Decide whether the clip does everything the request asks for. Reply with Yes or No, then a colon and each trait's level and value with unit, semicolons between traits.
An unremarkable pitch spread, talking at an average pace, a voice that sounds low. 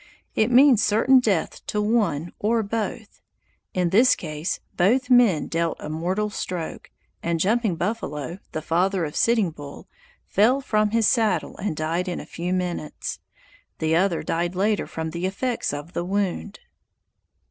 No: average, 4.6 semitones; average, 155 wpm; high, 190 Hz